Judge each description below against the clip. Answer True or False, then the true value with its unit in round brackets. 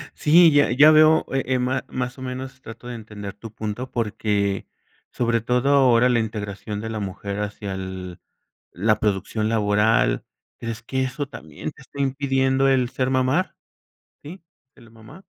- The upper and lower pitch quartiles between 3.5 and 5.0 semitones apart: True (4.0 semitones)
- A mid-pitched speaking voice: False (120 Hz)